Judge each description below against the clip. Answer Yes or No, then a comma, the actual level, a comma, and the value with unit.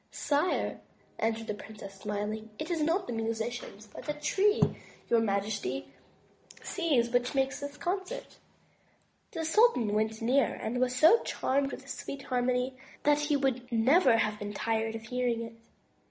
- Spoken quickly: No, average, 155 wpm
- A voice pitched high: Yes, high, 245 Hz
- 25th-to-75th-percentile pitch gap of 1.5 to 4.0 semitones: No, average, 4.8 semitones